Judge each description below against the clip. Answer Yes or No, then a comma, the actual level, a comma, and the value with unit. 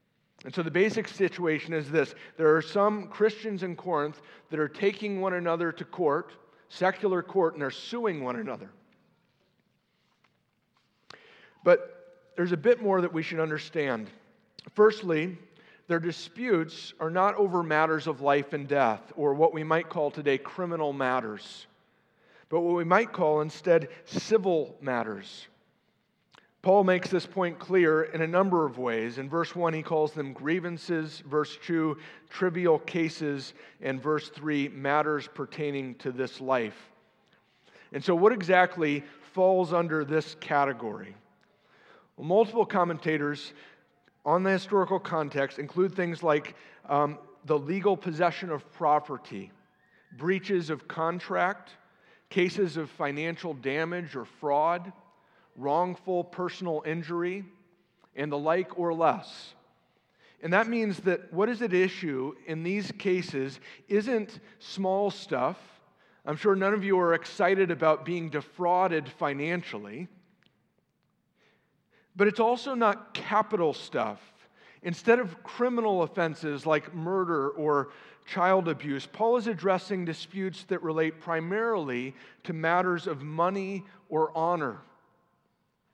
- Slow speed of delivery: Yes, slow, 130 wpm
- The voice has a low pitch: No, medium, 170 Hz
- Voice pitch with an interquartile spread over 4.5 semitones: No, average, 3.9 semitones